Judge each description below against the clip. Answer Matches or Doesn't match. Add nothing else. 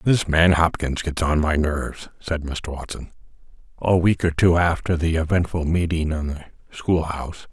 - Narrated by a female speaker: Doesn't match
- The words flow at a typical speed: Matches